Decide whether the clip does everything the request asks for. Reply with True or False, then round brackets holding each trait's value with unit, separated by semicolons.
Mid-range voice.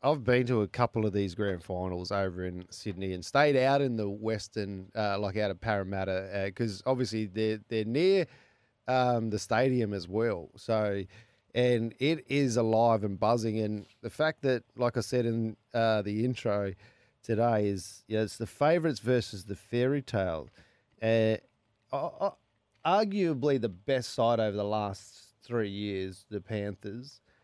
False (110 Hz)